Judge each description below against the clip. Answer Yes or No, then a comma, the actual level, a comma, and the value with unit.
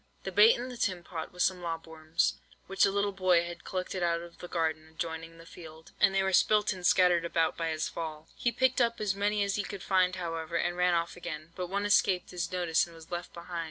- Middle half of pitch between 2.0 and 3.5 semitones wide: Yes, narrow, 2.6 semitones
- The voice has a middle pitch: Yes, medium, 175 Hz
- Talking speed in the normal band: No, fast, 245 wpm